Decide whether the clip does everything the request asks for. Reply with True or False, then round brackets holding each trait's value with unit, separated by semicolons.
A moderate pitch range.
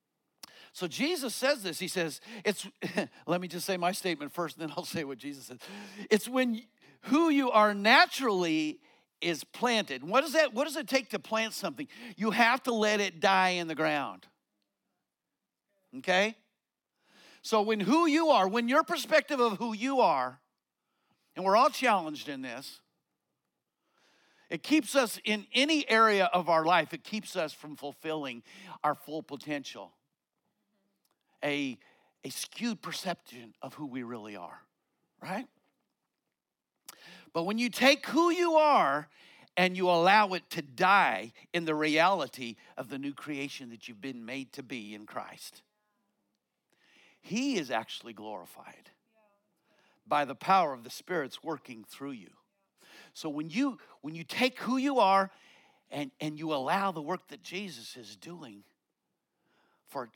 False (7.6 semitones)